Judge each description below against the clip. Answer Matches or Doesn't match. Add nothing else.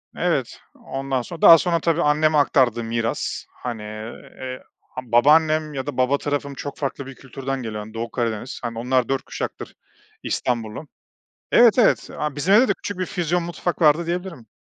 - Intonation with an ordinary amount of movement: Matches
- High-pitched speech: Doesn't match